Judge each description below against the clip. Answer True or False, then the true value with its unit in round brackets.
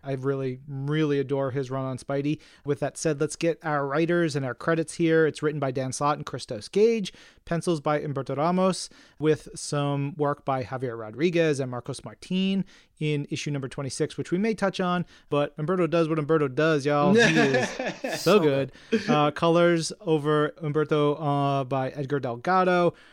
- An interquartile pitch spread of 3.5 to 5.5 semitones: False (3.1 semitones)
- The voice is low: False (150 Hz)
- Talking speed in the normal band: True (175 wpm)